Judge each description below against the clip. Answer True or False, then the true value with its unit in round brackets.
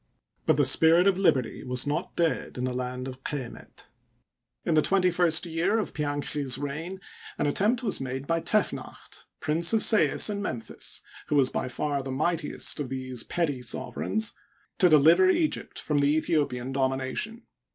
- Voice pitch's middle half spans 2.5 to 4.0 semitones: False (5.0 semitones)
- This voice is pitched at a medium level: True (150 Hz)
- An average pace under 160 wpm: False (165 wpm)